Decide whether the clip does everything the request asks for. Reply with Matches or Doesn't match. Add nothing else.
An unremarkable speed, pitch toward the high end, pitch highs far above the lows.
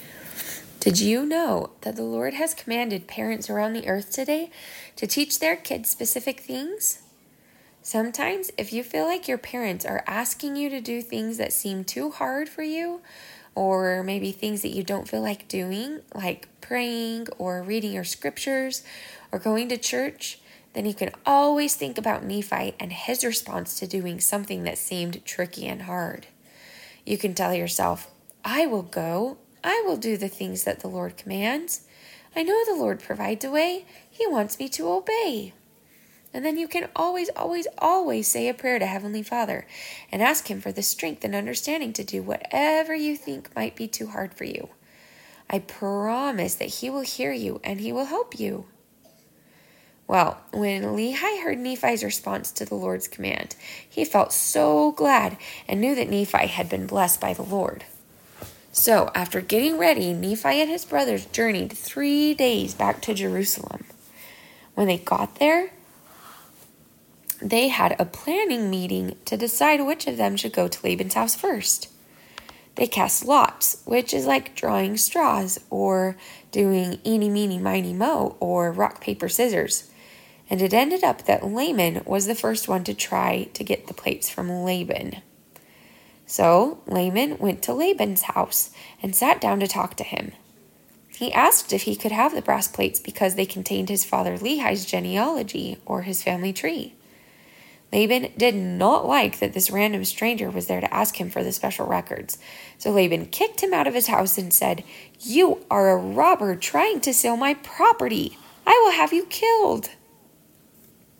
Matches